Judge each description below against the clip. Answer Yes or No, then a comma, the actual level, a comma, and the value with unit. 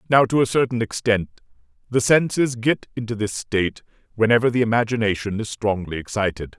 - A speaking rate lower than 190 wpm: Yes, average, 155 wpm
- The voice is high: No, low, 115 Hz